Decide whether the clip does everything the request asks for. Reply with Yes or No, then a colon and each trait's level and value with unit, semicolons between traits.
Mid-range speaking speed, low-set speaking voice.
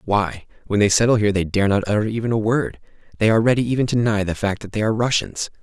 No: fast, 245 wpm; low, 105 Hz